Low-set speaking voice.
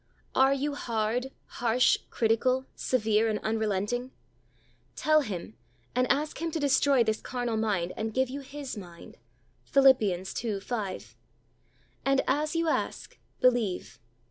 No: high, 245 Hz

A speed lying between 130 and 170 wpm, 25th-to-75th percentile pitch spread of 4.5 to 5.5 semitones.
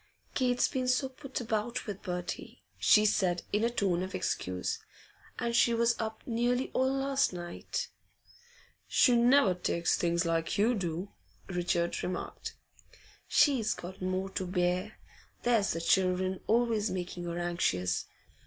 Yes: average, 140 wpm; average, 5.1 semitones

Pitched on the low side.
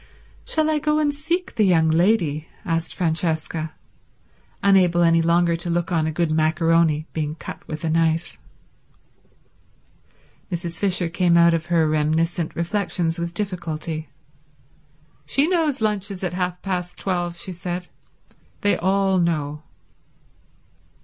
No: medium, 170 Hz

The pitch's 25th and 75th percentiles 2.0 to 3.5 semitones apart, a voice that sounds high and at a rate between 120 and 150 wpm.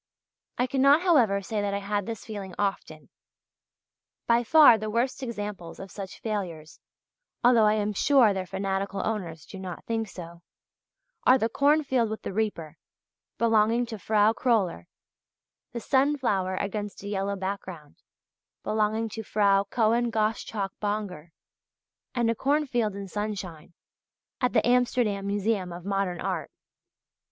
Yes: average, 3.1 semitones; high, 210 Hz; average, 140 wpm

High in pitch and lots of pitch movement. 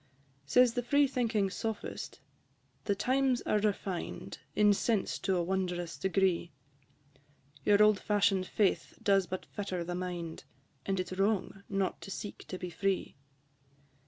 No: high, 195 Hz; narrow, 2.5 semitones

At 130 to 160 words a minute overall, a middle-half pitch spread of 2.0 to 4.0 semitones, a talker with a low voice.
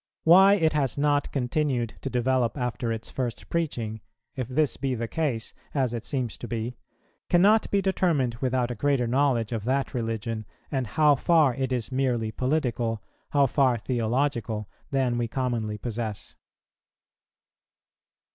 Yes: average, 145 wpm; average, 3.4 semitones; low, 125 Hz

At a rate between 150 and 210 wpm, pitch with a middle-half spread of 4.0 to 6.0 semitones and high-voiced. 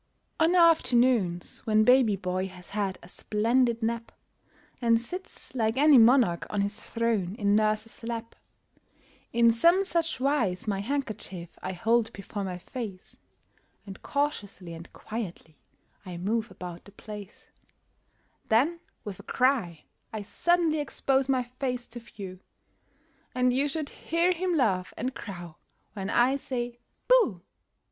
No: average, 140 wpm; average, 5.0 semitones; high, 230 Hz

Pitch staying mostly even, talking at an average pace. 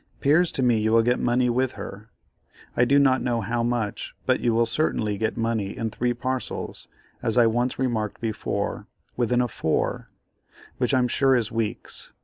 Yes: narrow, 1.9 semitones; average, 180 wpm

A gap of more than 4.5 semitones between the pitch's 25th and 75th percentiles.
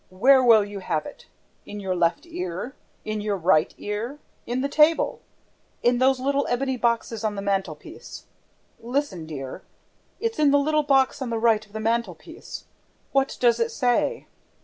Yes: average, 5.3 semitones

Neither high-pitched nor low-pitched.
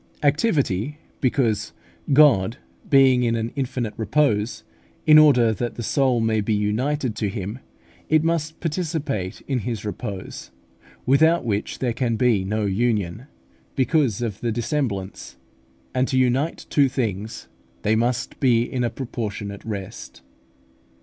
No: low, 120 Hz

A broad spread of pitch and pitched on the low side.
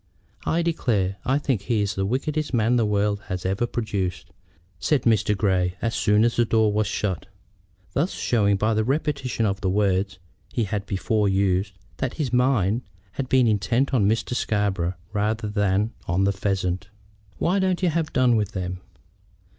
No: average, 4.0 semitones; low, 105 Hz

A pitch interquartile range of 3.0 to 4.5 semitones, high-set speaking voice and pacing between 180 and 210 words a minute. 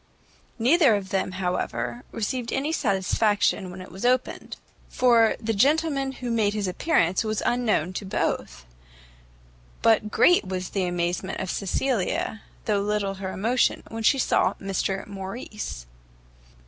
No: average, 4.2 semitones; high, 210 Hz; slow, 135 wpm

